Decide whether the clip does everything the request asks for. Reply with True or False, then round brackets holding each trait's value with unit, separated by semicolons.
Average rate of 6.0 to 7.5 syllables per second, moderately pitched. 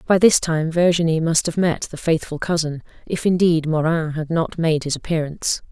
False (5.1 syllables/s; 160 Hz)